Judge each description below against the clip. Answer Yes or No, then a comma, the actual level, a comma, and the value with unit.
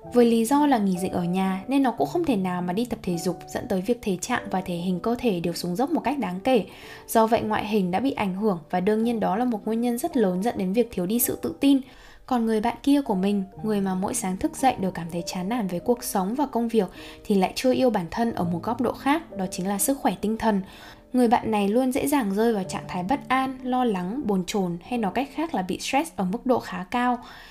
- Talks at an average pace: No, fast, 285 wpm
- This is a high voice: Yes, high, 225 Hz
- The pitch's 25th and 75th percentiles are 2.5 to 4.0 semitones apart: No, average, 4.7 semitones